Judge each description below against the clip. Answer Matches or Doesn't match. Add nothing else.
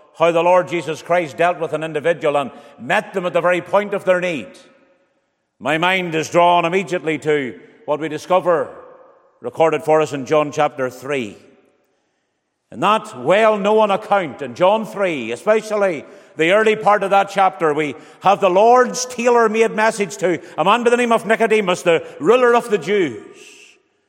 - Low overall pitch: Doesn't match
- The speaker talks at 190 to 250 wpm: Doesn't match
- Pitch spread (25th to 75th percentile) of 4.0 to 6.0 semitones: Matches